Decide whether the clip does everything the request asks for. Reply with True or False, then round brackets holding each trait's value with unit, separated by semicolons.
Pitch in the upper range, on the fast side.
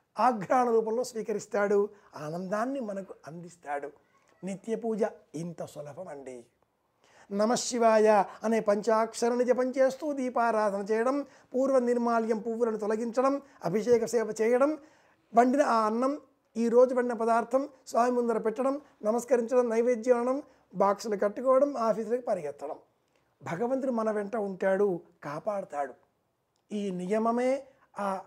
False (225 Hz; 100 wpm)